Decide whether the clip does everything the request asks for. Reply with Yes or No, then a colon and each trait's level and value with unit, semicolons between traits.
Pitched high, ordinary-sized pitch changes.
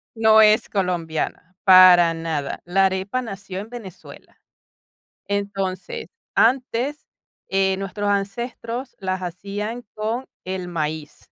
Yes: high, 195 Hz; average, 3.1 semitones